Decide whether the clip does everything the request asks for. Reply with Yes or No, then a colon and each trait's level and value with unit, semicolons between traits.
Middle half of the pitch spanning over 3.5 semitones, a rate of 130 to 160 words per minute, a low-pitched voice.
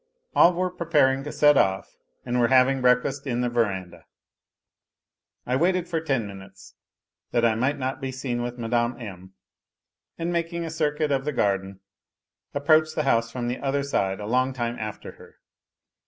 No: average, 4.2 semitones; average, 170 wpm; low, 130 Hz